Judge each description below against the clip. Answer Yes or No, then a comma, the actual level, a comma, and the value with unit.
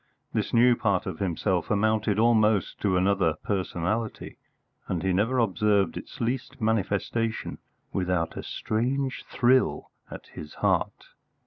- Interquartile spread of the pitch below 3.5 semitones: No, average, 3.8 semitones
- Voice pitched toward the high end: No, low, 105 Hz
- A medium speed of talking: No, slow, 125 wpm